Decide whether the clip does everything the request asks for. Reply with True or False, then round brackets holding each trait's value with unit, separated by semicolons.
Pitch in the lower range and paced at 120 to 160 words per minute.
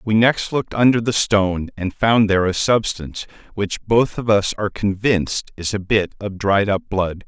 False (105 Hz; 200 wpm)